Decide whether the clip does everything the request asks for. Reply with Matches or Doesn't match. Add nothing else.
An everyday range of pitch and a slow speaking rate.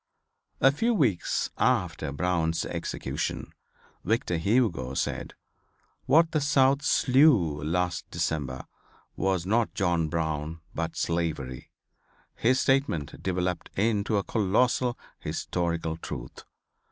Doesn't match